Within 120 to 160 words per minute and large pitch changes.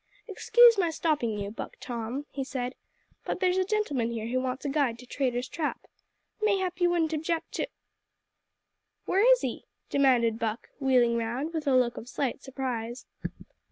No: average, 170 wpm; wide, 5.8 semitones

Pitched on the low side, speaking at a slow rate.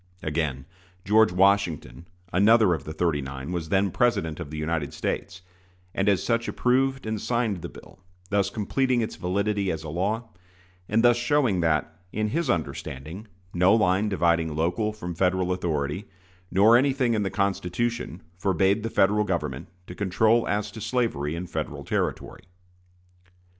No: very low, 95 Hz; average, 155 wpm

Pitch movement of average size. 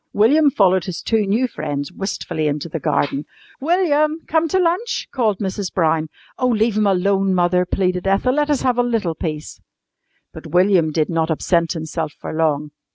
No: wide, 7.0 semitones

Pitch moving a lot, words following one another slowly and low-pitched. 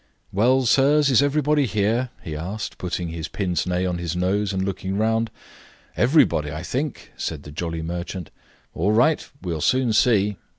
No: wide, 6.2 semitones; average, 165 wpm; low, 100 Hz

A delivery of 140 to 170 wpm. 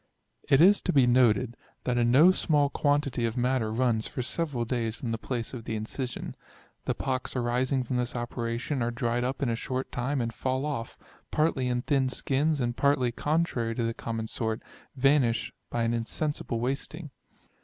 No: average, 185 wpm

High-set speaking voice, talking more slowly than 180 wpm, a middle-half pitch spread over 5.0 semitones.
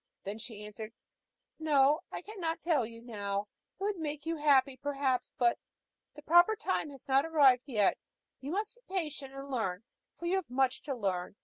No: very high, 275 Hz; average, 185 wpm; wide, 5.5 semitones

